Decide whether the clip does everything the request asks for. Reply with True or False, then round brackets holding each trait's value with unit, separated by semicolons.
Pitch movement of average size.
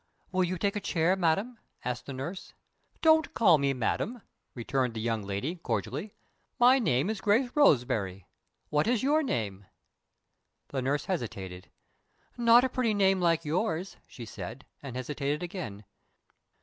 False (9.0 semitones)